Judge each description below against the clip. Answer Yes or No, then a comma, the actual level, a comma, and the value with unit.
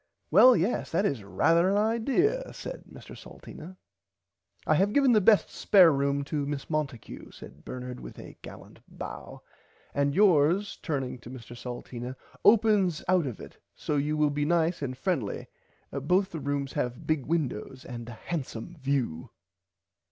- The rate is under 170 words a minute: Yes, average, 160 wpm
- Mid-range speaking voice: Yes, medium, 150 Hz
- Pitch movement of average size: No, wide, 6.1 semitones